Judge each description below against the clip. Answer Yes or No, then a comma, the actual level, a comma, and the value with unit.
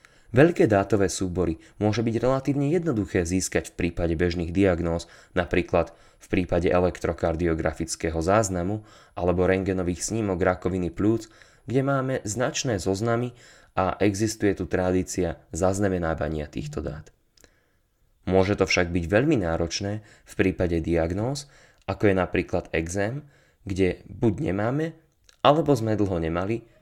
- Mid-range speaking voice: No, very low, 95 Hz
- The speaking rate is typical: Yes, average, 120 wpm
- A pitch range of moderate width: Yes, average, 4.2 semitones